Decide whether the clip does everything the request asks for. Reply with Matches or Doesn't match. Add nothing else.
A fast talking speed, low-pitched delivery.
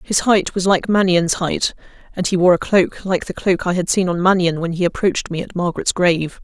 Doesn't match